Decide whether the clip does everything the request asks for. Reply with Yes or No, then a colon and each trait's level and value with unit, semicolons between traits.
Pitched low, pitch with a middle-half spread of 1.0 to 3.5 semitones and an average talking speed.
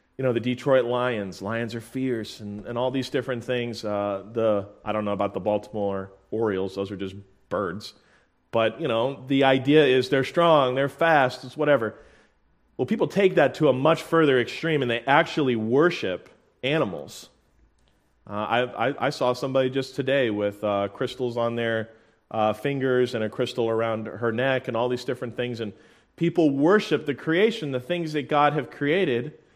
No: low, 125 Hz; average, 4.1 semitones; average, 185 wpm